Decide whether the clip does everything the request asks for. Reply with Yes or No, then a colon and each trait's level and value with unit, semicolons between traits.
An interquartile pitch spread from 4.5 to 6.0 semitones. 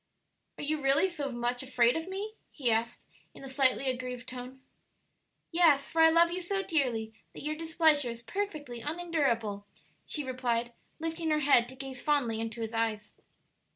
Yes: average, 5.1 semitones